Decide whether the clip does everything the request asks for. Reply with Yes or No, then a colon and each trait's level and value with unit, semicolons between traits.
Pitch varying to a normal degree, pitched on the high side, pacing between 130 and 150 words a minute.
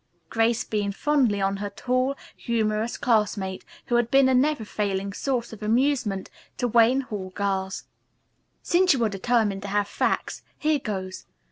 No: average, 4.0 semitones; high, 220 Hz; average, 160 wpm